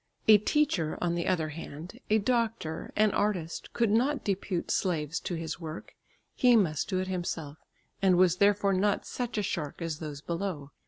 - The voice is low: No, medium, 185 Hz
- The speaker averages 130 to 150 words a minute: No, average, 175 wpm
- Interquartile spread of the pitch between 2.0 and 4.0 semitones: No, average, 4.4 semitones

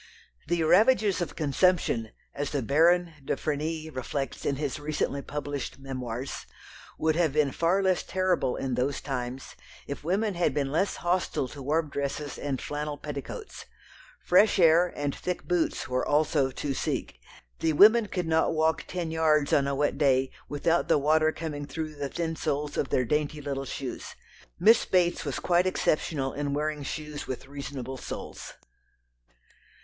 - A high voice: No, medium, 150 Hz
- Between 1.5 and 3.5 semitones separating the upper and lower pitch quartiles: Yes, average, 3.2 semitones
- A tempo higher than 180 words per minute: No, average, 160 wpm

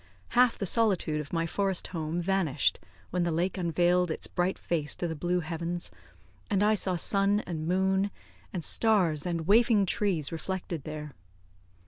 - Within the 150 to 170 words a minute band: Yes, average, 160 wpm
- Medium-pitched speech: Yes, medium, 175 Hz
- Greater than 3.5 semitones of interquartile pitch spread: No, average, 3.0 semitones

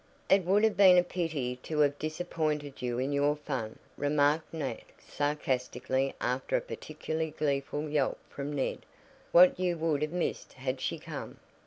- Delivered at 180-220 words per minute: No, average, 160 wpm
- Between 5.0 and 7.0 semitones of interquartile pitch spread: No, average, 2.9 semitones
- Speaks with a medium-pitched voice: Yes, medium, 150 Hz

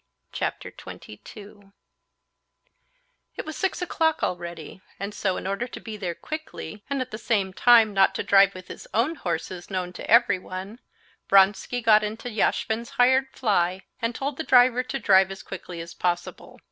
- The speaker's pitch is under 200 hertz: No, high, 210 Hz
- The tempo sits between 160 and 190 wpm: Yes, average, 165 wpm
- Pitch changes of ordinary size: Yes, average, 4.6 semitones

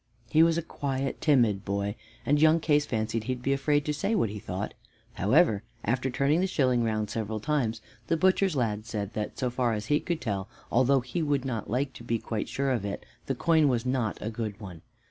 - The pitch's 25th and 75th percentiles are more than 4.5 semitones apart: Yes, average, 5.2 semitones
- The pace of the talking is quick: Yes, fast, 225 wpm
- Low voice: Yes, low, 125 Hz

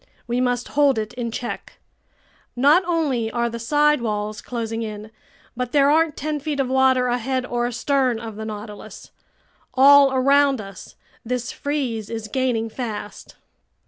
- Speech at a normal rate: Yes, average, 150 wpm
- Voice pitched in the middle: No, high, 245 Hz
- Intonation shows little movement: No, average, 3.6 semitones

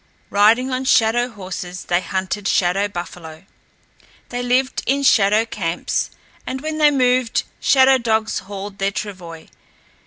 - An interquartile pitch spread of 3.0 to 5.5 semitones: Yes, average, 5.1 semitones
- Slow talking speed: Yes, slow, 130 wpm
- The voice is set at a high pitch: Yes, high, 210 Hz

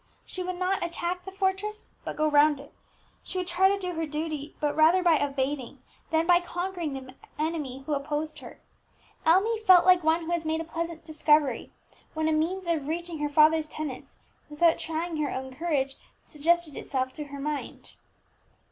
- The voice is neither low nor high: No, very high, 320 Hz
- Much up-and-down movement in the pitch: No, average, 2.9 semitones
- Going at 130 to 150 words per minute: No, average, 185 wpm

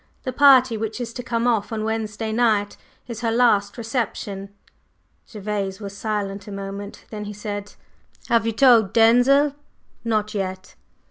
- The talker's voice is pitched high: Yes, high, 220 Hz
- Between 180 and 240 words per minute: No, average, 150 wpm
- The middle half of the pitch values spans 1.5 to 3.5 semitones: Yes, narrow, 2.4 semitones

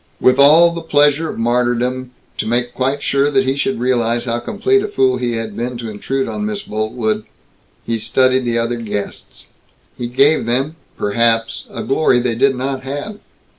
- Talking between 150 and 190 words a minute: Yes, average, 180 wpm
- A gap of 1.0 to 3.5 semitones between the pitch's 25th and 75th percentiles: Yes, average, 2.9 semitones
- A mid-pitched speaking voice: No, low, 125 Hz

